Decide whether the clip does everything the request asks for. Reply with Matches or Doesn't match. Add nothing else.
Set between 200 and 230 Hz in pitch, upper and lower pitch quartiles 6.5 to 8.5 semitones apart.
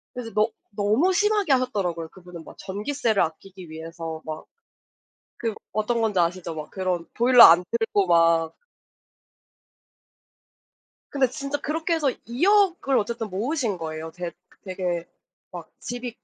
Matches